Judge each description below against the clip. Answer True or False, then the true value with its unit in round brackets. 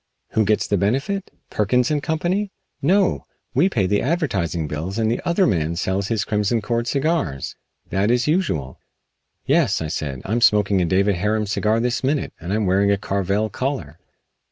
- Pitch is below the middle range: True (105 Hz)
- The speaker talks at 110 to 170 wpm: False (180 wpm)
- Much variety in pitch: True (5.8 semitones)